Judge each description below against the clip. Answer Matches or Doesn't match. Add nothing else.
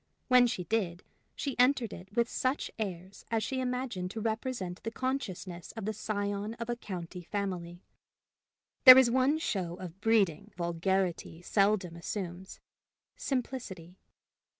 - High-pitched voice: Matches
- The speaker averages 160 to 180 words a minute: Doesn't match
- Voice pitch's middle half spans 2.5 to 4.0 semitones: Doesn't match